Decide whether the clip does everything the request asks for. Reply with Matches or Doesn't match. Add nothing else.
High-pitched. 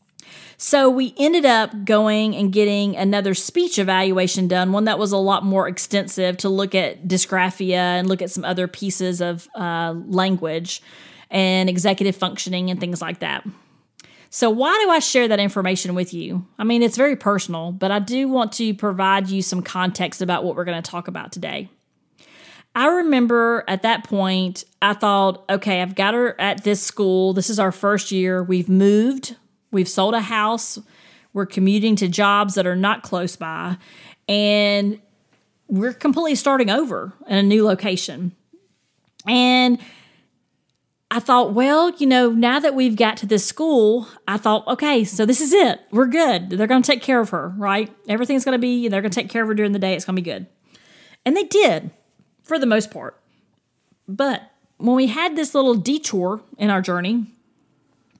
Matches